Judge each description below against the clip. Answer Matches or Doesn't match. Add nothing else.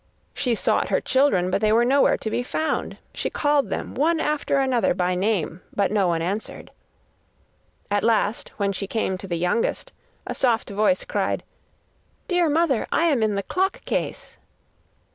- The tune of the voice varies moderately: Doesn't match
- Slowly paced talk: Doesn't match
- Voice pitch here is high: Matches